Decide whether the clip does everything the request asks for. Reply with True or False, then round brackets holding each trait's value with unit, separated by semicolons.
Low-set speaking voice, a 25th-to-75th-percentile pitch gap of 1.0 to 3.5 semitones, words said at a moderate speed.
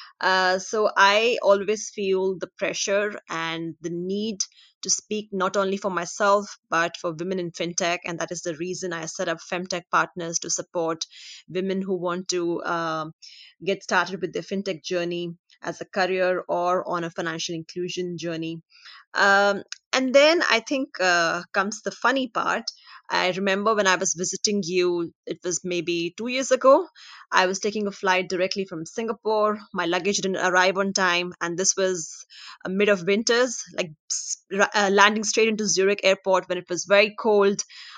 False (185 Hz; 2.4 semitones; 170 wpm)